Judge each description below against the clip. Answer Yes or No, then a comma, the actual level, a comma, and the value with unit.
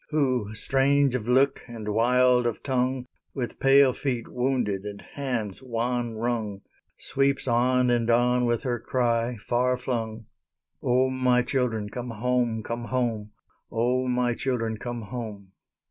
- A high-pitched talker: No, low, 120 Hz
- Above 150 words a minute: No, average, 140 wpm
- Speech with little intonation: Yes, narrow, 1.8 semitones